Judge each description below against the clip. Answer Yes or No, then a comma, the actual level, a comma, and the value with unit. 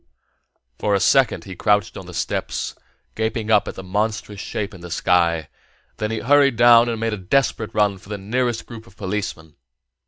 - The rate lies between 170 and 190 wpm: No, average, 200 wpm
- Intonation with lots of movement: No, average, 2.9 semitones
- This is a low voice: Yes, low, 105 Hz